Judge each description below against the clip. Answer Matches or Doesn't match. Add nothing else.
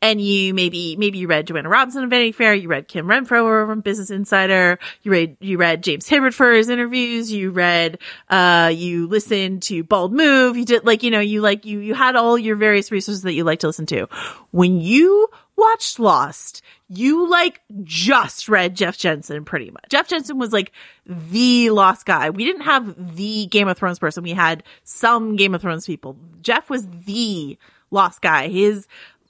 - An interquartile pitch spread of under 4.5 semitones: Doesn't match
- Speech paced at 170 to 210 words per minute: Matches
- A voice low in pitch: Doesn't match